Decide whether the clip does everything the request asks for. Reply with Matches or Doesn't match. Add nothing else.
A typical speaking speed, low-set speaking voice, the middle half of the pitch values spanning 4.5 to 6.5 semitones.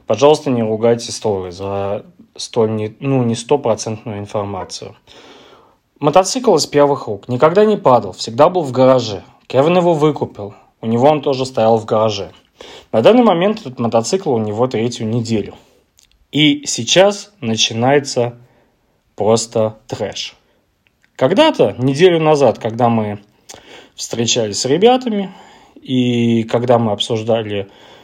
Matches